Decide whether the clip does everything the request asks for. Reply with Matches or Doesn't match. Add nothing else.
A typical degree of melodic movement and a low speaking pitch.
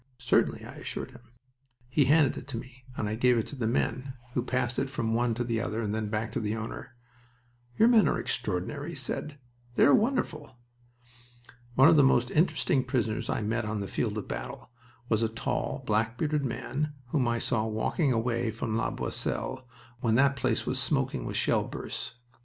Matches